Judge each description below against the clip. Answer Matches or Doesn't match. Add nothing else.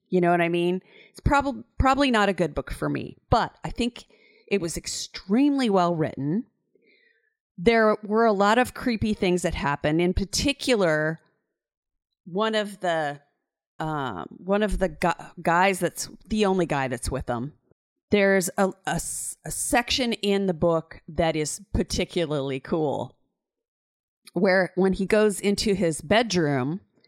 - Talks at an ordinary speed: Matches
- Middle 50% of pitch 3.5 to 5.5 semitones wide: Matches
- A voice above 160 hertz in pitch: Matches